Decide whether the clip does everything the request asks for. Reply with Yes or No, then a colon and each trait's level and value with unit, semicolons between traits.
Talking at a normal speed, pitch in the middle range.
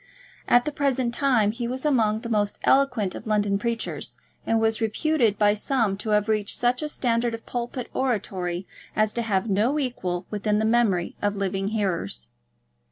No: average, 180 wpm; high, 220 Hz